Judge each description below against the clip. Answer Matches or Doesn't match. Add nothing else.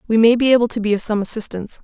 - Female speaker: Matches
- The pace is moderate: Doesn't match